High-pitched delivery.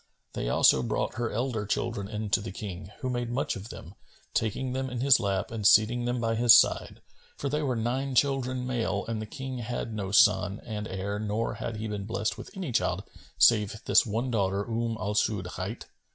No: low, 115 Hz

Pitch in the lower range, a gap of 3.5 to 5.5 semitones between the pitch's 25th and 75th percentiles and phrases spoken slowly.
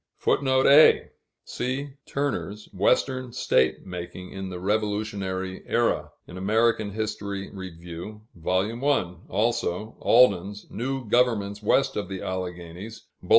Yes: low, 105 Hz; average, 4.1 semitones; slow, 115 wpm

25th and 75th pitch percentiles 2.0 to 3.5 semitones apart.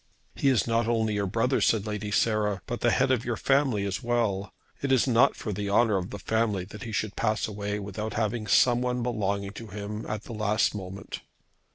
Yes: narrow, 2.6 semitones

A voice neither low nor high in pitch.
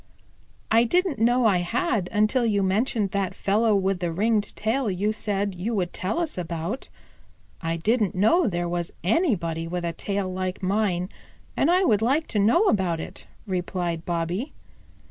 No: high, 200 Hz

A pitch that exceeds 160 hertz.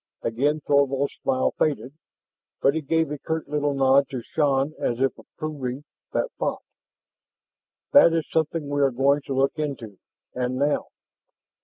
No: medium, 140 Hz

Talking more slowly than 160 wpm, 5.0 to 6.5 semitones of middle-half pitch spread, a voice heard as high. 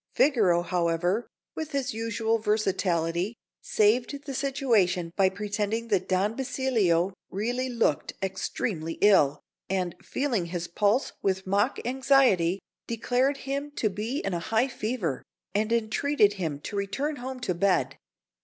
Yes: slow, 135 wpm; average, 5.3 semitones; high, 210 Hz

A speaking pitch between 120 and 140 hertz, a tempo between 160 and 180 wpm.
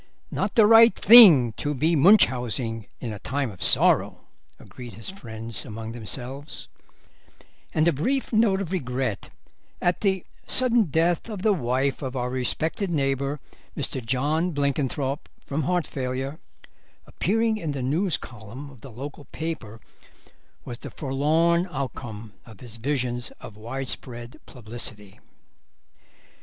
No: low, 135 Hz; slow, 135 wpm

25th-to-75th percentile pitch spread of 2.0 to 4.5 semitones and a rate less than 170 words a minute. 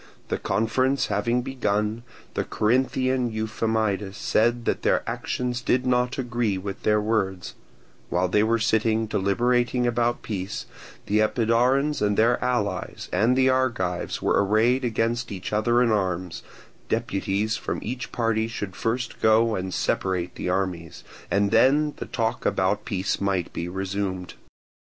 Yes: average, 3.6 semitones; average, 140 wpm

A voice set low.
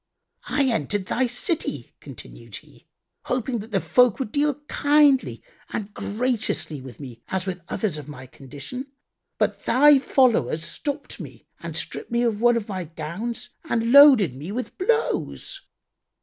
No: high, 225 Hz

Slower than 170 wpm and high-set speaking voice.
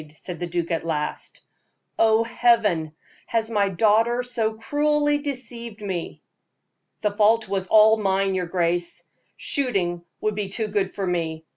Yes: average, 150 wpm; high, 210 Hz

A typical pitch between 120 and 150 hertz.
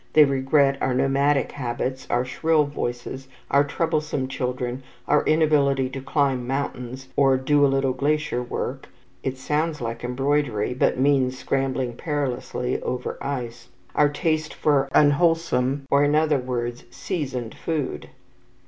Yes: low, 135 Hz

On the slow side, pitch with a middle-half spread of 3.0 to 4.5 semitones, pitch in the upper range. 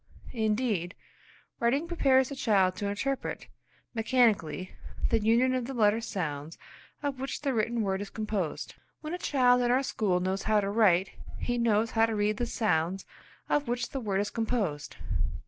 No: average, 170 wpm; average, 4.0 semitones; high, 225 Hz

